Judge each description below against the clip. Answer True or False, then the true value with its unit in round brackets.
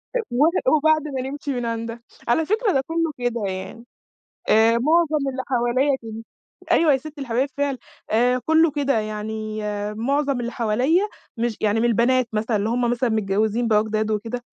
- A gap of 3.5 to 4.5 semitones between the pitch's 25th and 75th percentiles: True (4.2 semitones)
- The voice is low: False (240 Hz)